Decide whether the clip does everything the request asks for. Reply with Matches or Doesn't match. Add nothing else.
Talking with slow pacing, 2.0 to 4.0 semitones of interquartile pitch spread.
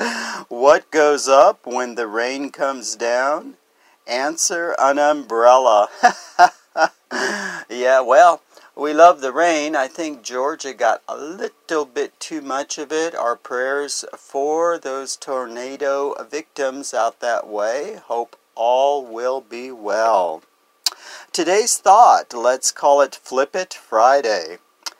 Matches